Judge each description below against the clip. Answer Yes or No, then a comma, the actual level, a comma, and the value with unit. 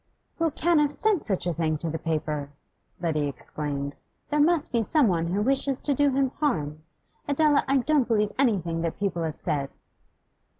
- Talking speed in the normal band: Yes, average, 175 wpm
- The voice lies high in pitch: Yes, high, 205 Hz